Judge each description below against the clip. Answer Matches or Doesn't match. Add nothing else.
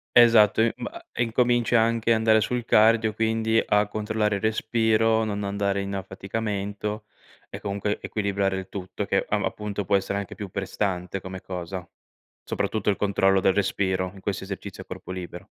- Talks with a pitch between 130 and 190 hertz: Doesn't match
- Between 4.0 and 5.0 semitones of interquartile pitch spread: Doesn't match